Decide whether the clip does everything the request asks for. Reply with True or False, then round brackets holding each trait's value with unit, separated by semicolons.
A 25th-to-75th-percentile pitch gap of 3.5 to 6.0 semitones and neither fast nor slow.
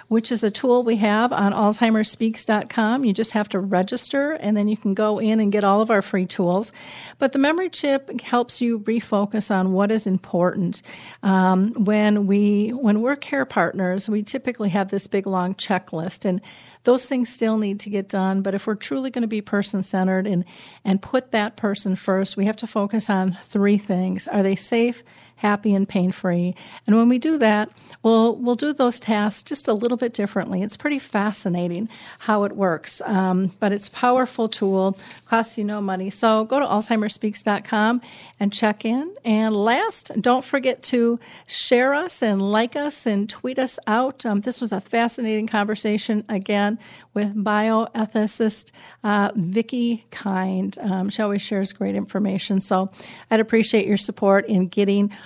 False (2.8 semitones; 175 wpm)